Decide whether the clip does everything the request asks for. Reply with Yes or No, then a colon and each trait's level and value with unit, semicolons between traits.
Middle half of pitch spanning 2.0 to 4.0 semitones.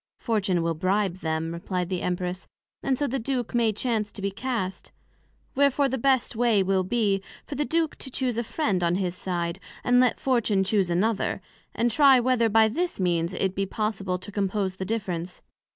No: average, 4.8 semitones